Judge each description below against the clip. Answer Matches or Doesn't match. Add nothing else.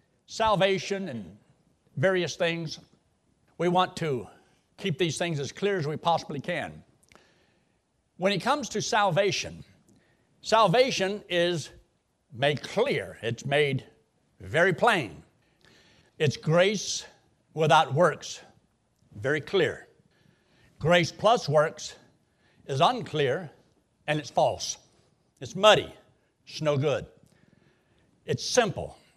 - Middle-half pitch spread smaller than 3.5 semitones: Doesn't match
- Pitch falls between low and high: Matches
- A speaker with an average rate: Doesn't match